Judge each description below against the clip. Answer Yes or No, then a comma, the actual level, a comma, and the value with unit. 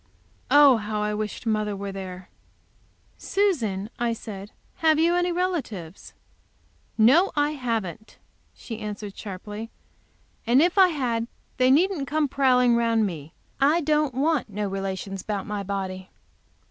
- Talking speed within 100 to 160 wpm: Yes, slow, 135 wpm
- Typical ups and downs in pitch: No, wide, 6.4 semitones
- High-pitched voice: Yes, high, 230 Hz